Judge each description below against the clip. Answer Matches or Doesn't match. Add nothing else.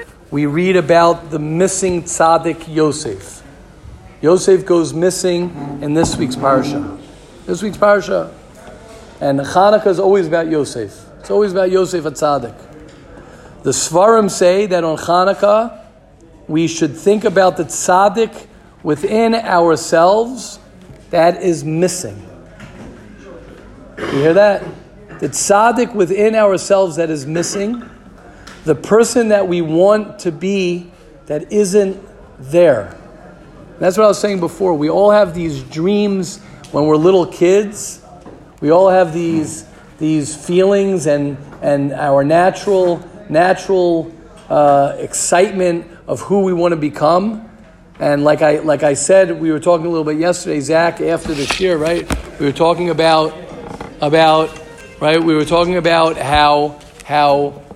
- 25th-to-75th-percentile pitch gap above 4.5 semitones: Doesn't match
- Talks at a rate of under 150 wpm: Matches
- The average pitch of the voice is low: Doesn't match